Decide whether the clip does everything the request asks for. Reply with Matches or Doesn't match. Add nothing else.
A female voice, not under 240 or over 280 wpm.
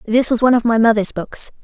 Matches